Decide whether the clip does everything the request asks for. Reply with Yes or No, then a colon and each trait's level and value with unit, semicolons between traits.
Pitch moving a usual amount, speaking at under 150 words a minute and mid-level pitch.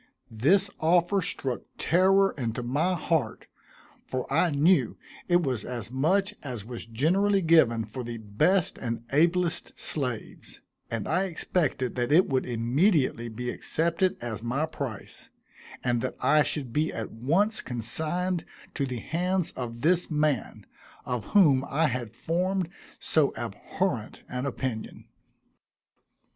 No: wide, 6.4 semitones; slow, 135 wpm; medium, 145 Hz